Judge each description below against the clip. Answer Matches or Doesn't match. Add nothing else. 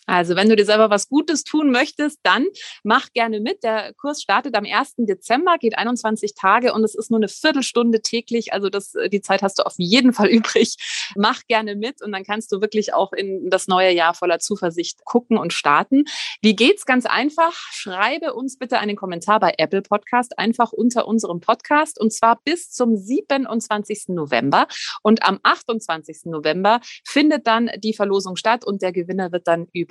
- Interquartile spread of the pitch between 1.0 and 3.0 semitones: Doesn't match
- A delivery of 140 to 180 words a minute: Doesn't match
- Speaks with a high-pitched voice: Matches